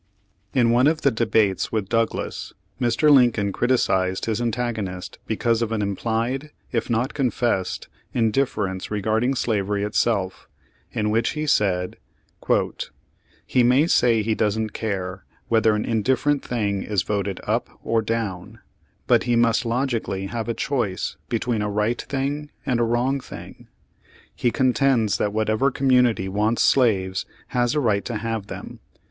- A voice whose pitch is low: Yes, low, 115 Hz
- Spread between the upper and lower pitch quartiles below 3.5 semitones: Yes, average, 2.9 semitones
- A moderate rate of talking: Yes, average, 145 wpm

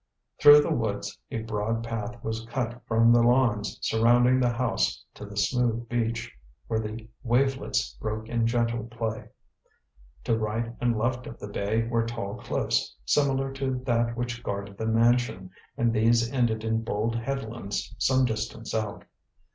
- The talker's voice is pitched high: No, low, 115 Hz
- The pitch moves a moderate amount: No, narrow, 1.5 semitones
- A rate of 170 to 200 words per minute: No, average, 155 wpm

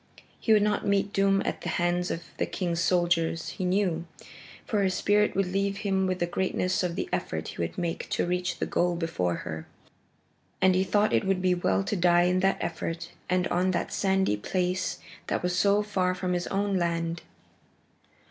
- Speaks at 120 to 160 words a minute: No, average, 195 wpm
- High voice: No, medium, 180 Hz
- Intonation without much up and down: Yes, narrow, 2.0 semitones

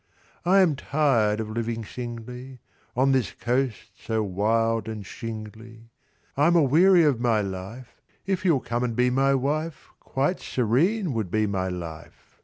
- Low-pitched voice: Yes, low, 120 Hz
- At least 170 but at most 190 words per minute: No, average, 155 wpm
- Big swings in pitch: No, average, 3.9 semitones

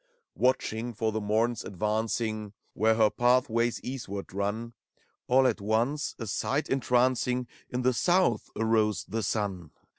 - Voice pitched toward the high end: No, low, 115 Hz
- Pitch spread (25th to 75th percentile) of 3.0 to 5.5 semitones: No, narrow, 2.6 semitones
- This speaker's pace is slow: Yes, slow, 130 wpm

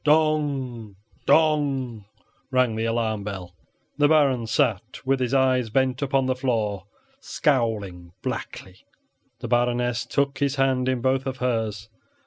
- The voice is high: No, low, 125 Hz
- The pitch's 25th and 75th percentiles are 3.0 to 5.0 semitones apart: Yes, average, 3.3 semitones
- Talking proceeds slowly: Yes, slow, 130 wpm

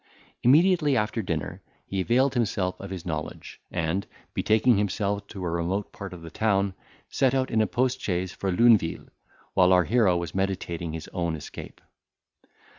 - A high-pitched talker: No, very low, 95 Hz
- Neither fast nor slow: Yes, average, 165 wpm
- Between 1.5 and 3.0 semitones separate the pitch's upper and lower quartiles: No, average, 4.3 semitones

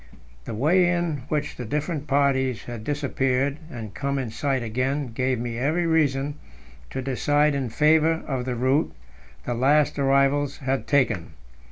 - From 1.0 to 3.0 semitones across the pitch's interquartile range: Yes, average, 2.7 semitones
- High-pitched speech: No, low, 135 Hz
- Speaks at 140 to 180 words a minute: Yes, average, 155 wpm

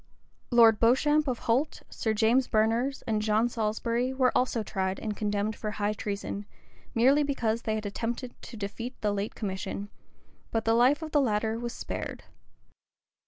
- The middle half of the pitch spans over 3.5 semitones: No, average, 2.8 semitones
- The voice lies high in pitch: Yes, high, 225 Hz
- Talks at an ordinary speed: Yes, average, 165 wpm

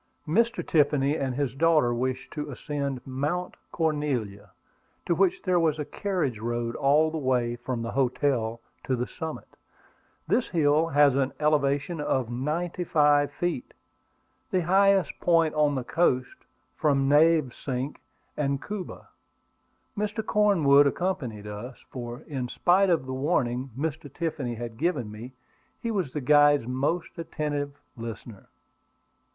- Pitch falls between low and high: Yes, medium, 145 Hz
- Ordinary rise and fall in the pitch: Yes, average, 4.4 semitones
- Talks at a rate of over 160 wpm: No, slow, 135 wpm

